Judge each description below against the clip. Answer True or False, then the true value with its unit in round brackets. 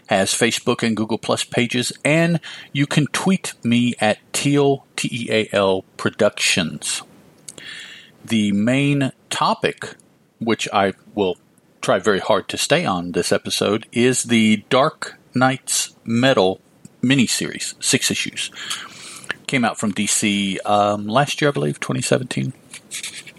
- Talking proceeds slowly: True (120 wpm)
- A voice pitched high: False (115 Hz)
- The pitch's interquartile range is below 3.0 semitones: False (4.2 semitones)